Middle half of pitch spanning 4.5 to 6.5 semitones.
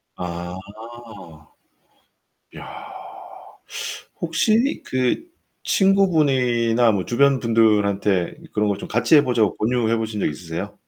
Yes: wide, 5.4 semitones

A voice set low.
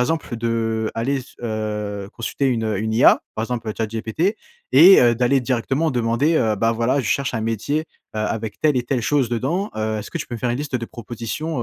Yes: low, 120 Hz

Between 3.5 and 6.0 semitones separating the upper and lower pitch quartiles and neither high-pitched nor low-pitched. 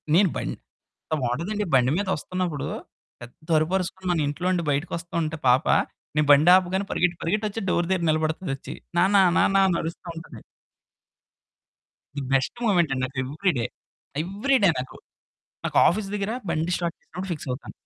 Yes: average, 4.0 semitones; medium, 170 Hz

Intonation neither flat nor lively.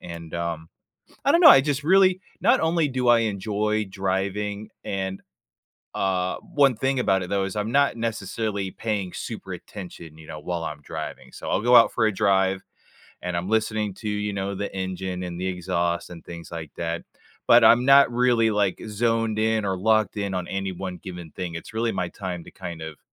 Yes: average, 3.7 semitones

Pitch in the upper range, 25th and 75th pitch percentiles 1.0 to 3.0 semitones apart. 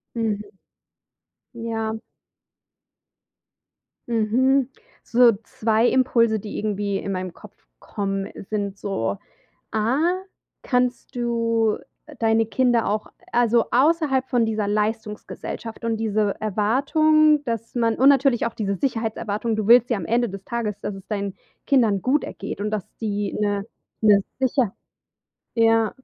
Yes: high, 225 Hz; narrow, 2.6 semitones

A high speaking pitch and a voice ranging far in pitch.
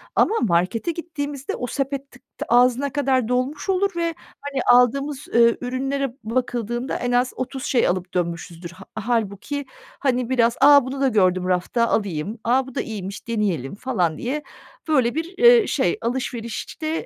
No: high, 245 Hz; average, 4.2 semitones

